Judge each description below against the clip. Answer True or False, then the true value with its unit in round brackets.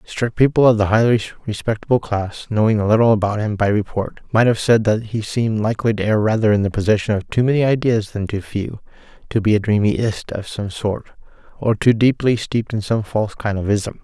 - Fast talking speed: True (220 wpm)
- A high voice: False (110 Hz)